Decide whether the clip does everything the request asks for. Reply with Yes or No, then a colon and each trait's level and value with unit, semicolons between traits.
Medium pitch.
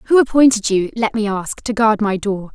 No: high, 215 Hz